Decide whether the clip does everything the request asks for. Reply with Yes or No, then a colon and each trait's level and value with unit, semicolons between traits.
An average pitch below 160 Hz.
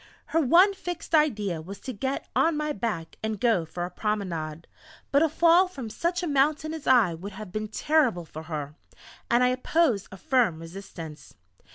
No: high, 225 Hz